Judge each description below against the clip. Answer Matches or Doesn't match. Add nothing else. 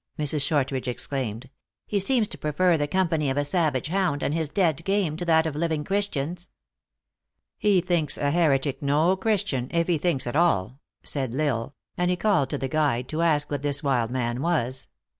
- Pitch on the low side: Doesn't match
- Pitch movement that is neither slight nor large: Matches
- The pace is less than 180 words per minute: Doesn't match